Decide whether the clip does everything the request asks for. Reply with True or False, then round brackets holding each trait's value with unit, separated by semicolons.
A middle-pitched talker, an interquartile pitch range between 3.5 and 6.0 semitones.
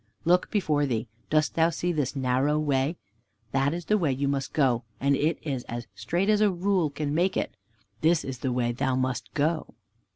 True (145 Hz; 4.2 semitones)